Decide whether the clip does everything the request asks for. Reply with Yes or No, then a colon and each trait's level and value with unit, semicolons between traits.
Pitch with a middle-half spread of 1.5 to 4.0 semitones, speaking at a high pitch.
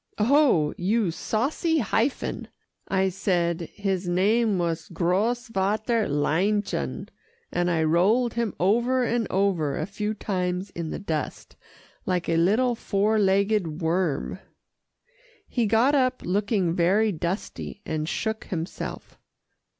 No: average, 4.4 semitones; high, 195 Hz